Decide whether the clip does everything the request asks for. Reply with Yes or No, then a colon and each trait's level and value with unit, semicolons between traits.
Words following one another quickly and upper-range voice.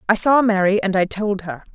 Yes: fast, 240 wpm; high, 200 Hz